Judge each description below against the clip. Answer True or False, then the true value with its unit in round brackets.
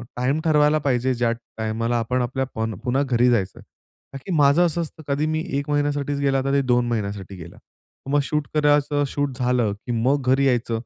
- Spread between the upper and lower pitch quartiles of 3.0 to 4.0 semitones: True (3.4 semitones)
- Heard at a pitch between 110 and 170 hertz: True (135 Hz)